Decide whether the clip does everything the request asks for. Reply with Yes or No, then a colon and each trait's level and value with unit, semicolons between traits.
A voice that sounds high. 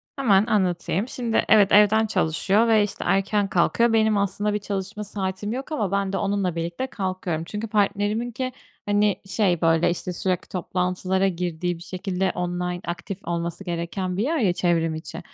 Yes: high, 195 Hz